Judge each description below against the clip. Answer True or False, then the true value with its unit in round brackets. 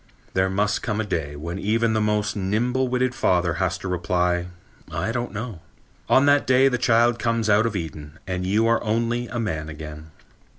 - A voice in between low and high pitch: False (105 Hz)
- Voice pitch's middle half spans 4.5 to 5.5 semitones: True (4.8 semitones)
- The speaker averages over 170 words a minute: True (195 wpm)